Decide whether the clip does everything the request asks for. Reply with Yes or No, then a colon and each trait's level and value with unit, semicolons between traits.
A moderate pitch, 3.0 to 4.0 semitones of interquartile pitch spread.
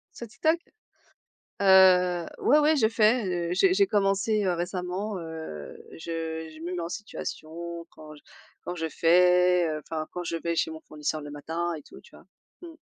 Yes: medium, 175 Hz; average, 3.4 semitones